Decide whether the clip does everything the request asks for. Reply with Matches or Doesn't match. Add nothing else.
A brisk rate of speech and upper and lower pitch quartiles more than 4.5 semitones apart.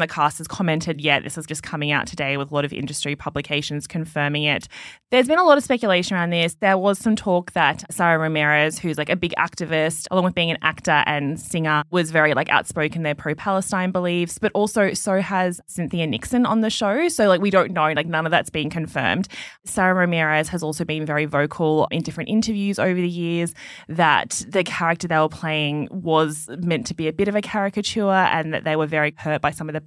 Doesn't match